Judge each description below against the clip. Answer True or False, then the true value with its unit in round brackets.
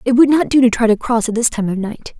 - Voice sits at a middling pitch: False (235 Hz)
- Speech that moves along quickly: True (355 wpm)